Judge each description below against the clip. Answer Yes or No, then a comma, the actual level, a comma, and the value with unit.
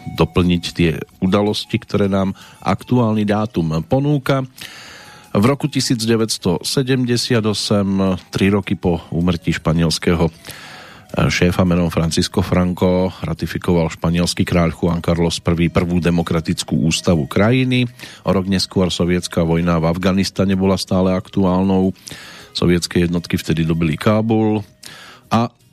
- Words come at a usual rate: No, slow, 105 wpm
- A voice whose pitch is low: Yes, very low, 95 Hz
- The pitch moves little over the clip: No, average, 3.7 semitones